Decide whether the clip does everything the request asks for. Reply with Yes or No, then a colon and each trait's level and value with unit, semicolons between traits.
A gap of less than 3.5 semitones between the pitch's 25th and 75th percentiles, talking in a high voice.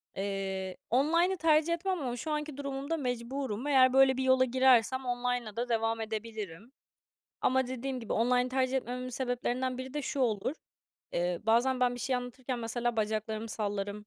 Yes: average, 2.9 semitones; very high, 250 Hz